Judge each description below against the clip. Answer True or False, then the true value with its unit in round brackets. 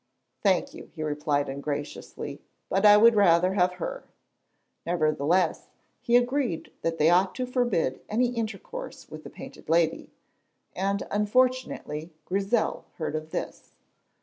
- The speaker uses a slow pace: True (130 wpm)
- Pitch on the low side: False (190 Hz)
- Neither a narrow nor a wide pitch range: False (6.5 semitones)